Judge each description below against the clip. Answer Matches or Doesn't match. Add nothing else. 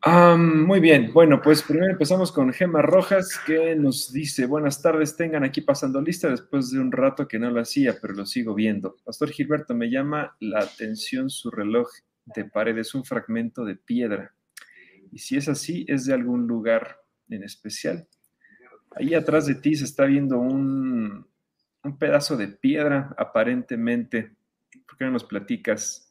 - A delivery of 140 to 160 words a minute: Doesn't match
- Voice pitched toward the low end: Doesn't match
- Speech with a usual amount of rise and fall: Doesn't match